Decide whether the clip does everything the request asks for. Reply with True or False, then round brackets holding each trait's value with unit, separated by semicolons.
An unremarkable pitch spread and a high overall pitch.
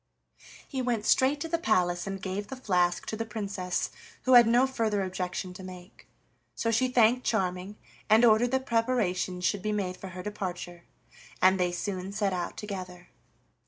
True (4.0 semitones; 200 Hz)